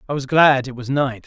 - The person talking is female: No, male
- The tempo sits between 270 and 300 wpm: Yes, fast, 285 wpm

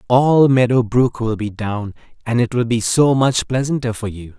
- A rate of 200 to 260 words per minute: Yes, fast, 205 wpm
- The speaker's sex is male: Yes, male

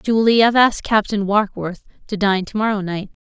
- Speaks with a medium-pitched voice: No, high, 205 Hz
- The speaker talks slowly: No, fast, 205 wpm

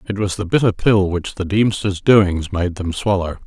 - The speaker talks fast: Yes, fast, 210 wpm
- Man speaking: Yes, male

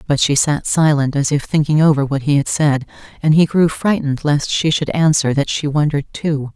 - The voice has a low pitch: No, medium, 145 Hz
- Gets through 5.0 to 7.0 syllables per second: Yes, 5.3 syllables/s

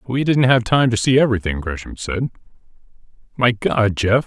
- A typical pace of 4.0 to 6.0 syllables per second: Yes, 5.1 syllables/s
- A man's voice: Yes, male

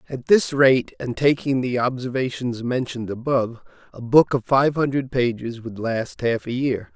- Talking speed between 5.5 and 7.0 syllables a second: No, 4.7 syllables/s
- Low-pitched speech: Yes, low, 125 Hz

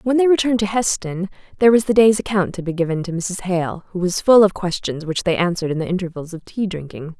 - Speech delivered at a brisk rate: Yes, fast, 250 wpm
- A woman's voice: Yes, female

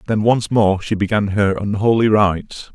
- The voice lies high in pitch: No, low, 105 Hz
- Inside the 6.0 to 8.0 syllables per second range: No, 4.7 syllables/s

